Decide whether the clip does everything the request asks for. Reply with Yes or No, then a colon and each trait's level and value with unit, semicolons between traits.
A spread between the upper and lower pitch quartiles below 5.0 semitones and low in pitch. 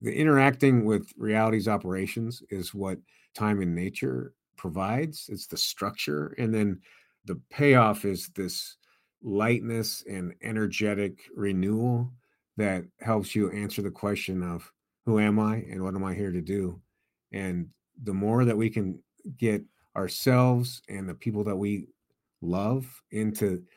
Yes: average, 3.0 semitones; low, 105 Hz